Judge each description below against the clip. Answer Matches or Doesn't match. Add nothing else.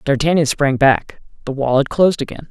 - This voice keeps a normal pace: Matches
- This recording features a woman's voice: Doesn't match